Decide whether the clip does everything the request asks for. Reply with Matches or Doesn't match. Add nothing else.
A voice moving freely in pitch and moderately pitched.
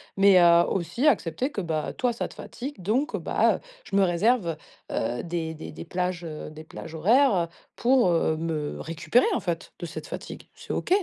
Matches